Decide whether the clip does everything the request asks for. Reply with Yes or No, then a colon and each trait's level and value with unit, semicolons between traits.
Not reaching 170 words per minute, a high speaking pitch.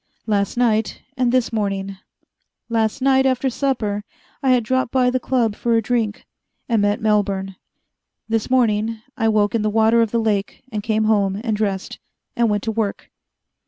No: average, 175 wpm; high, 220 Hz